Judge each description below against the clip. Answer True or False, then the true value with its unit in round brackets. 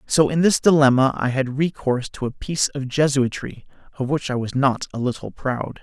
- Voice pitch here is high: False (135 Hz)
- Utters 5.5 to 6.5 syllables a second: False (5.3 syllables/s)